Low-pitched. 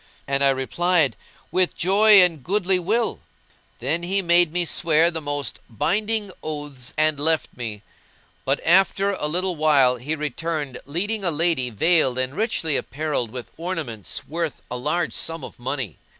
No: medium, 160 Hz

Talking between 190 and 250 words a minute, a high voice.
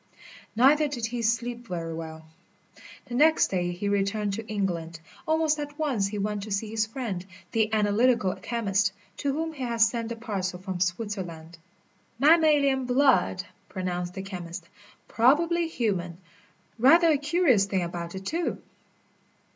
No: average, 145 wpm; high, 220 Hz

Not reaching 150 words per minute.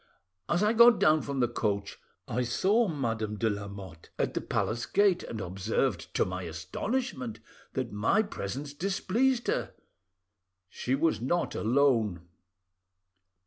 Yes: slow, 135 wpm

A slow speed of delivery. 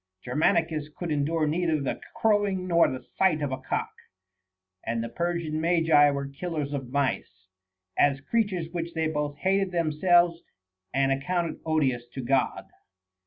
No: average, 150 wpm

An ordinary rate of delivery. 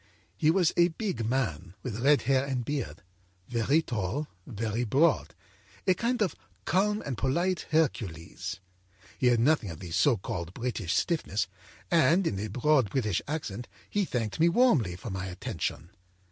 Yes: average, 160 wpm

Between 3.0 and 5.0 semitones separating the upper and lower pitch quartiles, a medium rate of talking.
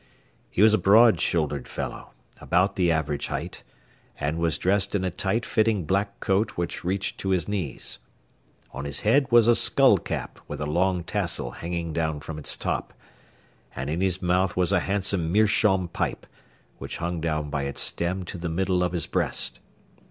Yes: average, 3.3 semitones; average, 180 wpm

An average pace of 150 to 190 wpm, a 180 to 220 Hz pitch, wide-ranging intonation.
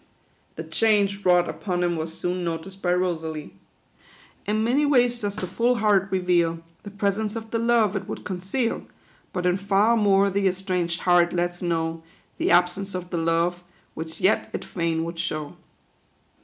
No: average, 170 wpm; medium, 185 Hz; average, 3.0 semitones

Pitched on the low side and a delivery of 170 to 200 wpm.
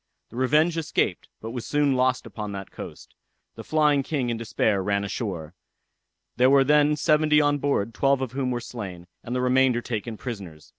Yes: low, 125 Hz; average, 185 wpm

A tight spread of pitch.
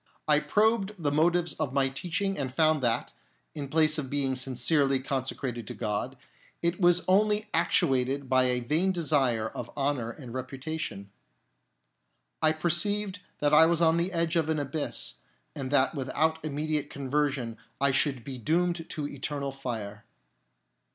No: average, 3.8 semitones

